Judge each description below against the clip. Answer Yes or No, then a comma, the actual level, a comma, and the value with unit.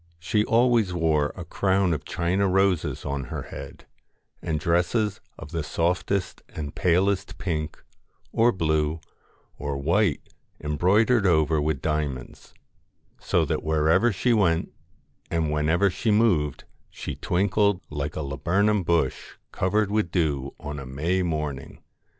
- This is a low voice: Yes, very low, 85 Hz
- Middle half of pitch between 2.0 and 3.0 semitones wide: No, average, 4.5 semitones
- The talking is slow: Yes, slow, 130 wpm